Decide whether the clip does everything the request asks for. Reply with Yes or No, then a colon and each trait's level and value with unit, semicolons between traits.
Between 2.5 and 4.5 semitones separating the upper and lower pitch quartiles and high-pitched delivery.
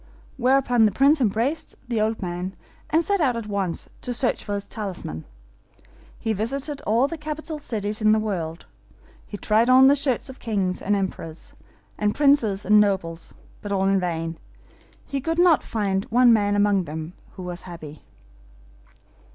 No: average, 5.3 semitones; high, 215 Hz